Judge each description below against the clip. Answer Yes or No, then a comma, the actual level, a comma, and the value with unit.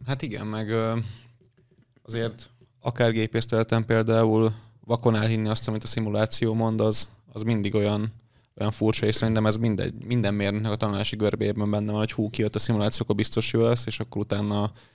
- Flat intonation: Yes, narrow, 1.3 semitones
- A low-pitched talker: Yes, low, 110 Hz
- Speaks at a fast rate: Yes, fast, 175 wpm